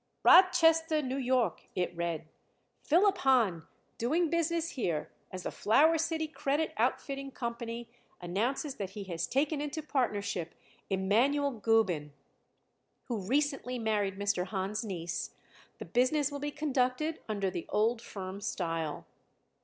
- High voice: Yes, high, 240 Hz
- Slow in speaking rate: Yes, slow, 130 wpm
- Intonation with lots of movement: Yes, wide, 7.1 semitones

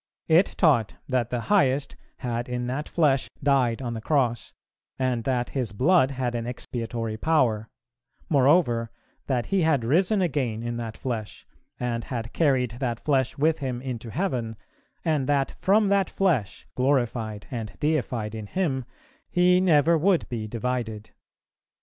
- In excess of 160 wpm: No, average, 150 wpm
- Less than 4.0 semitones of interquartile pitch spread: No, average, 4.4 semitones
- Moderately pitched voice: No, low, 130 Hz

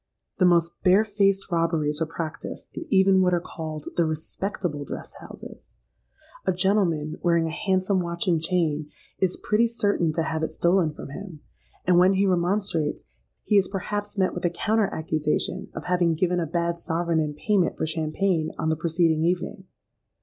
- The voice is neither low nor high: Yes, medium, 175 Hz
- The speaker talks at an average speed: Yes, average, 175 wpm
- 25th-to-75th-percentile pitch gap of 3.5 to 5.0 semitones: No, average, 3.0 semitones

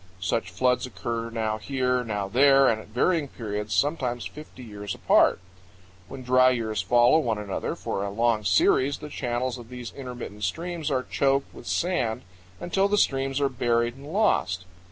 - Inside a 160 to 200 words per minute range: Yes, average, 170 wpm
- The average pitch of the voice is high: No, low, 125 Hz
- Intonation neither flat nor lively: Yes, average, 3.9 semitones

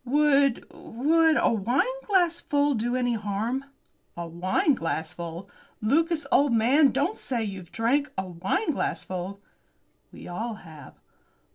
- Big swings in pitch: Yes, wide, 7.1 semitones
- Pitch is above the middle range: Yes, high, 240 Hz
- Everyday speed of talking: No, slow, 110 wpm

